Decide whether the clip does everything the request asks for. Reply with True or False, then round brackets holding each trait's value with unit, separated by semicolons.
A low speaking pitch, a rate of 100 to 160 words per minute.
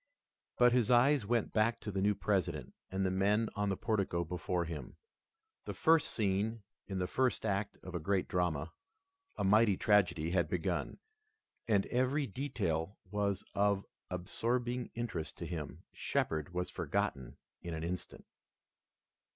True (100 Hz; 150 wpm)